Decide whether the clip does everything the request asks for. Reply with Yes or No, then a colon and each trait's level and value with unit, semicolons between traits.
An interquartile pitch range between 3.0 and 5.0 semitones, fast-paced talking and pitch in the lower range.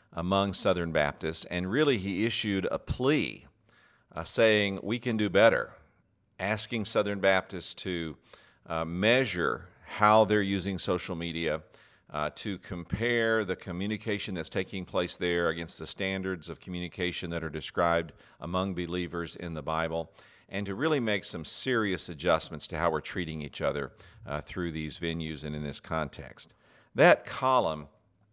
No: average, 3.5 semitones; average, 150 wpm; very low, 90 Hz